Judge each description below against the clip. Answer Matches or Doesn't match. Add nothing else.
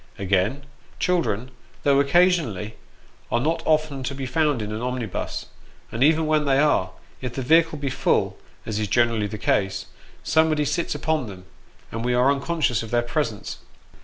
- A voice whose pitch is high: Doesn't match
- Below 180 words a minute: Matches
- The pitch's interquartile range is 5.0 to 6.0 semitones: Matches